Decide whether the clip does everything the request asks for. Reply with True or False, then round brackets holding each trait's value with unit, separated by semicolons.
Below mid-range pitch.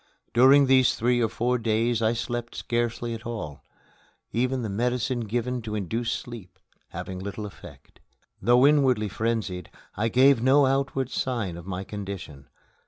True (115 Hz)